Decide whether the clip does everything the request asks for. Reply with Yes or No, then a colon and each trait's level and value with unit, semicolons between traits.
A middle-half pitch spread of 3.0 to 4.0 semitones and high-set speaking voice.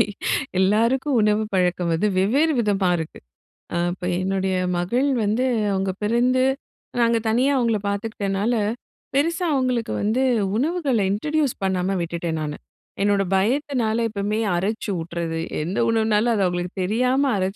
No: average, 4.7 semitones; high, 210 Hz